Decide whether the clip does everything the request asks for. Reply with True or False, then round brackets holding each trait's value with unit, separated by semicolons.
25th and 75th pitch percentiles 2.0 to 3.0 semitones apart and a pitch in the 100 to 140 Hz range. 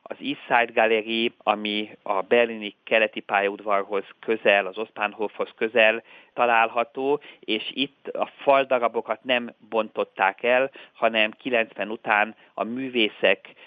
True (2.4 semitones; 110 Hz)